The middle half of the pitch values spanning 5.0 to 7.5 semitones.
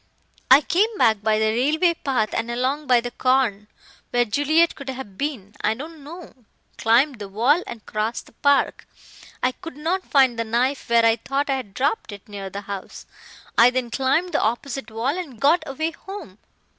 No: average, 4.6 semitones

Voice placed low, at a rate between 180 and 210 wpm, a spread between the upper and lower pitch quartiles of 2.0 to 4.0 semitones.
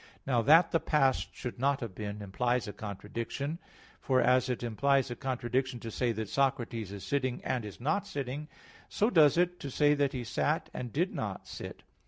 Yes: low, 130 Hz; average, 195 wpm; average, 3.5 semitones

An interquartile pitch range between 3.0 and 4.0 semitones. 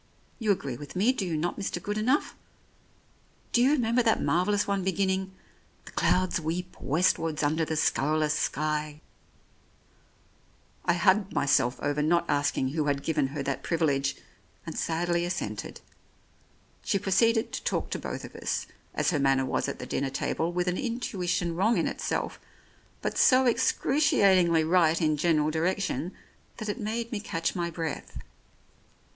No: average, 4.8 semitones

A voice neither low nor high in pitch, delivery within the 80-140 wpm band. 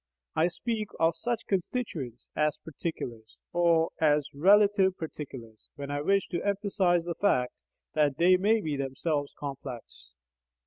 Yes: medium, 165 Hz; slow, 135 wpm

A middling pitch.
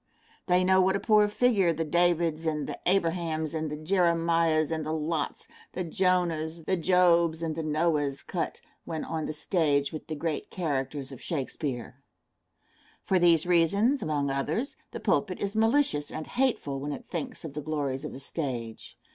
Yes: medium, 165 Hz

